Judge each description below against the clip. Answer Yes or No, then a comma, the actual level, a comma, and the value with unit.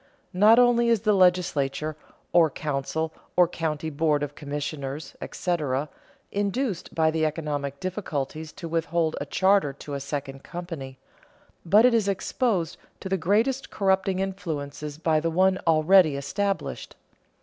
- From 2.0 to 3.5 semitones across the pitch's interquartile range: No, average, 4.6 semitones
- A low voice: No, medium, 165 Hz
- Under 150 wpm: Yes, average, 140 wpm